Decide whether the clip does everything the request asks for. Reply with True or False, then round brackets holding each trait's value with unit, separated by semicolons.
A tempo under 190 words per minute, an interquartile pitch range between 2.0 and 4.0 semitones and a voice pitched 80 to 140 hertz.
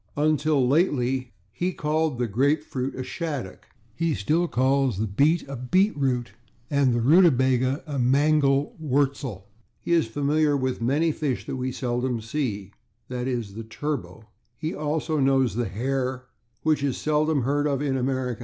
True (155 wpm; 3.4 semitones; 135 Hz)